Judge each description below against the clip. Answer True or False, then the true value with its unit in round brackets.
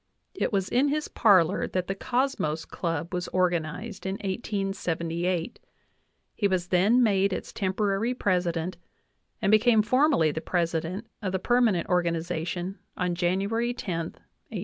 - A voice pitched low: False (190 Hz)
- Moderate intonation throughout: True (3.6 semitones)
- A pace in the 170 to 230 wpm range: False (145 wpm)